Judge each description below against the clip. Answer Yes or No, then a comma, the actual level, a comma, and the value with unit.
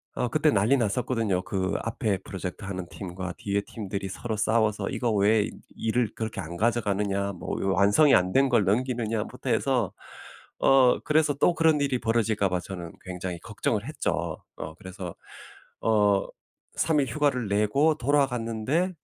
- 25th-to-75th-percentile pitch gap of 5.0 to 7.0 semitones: No, average, 4.4 semitones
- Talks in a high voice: No, low, 110 Hz